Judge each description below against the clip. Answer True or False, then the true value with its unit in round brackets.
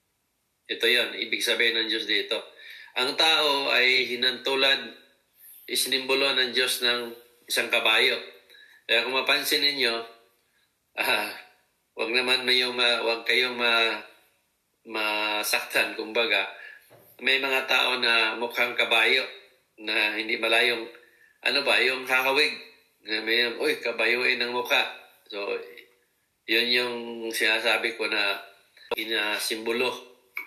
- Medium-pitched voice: False (120 Hz)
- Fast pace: False (115 wpm)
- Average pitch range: False (2.3 semitones)